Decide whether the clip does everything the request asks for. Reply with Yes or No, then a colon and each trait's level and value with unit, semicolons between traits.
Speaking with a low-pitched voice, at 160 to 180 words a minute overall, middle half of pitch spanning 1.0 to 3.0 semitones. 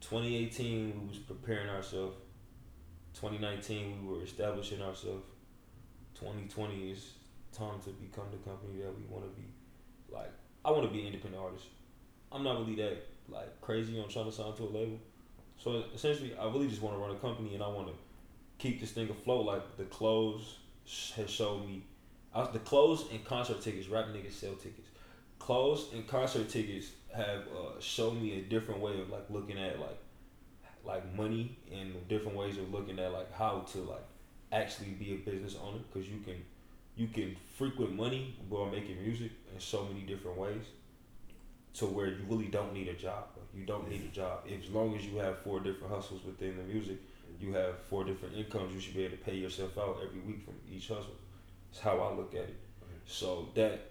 No: low, 100 Hz; average, 200 wpm; narrow, 2.6 semitones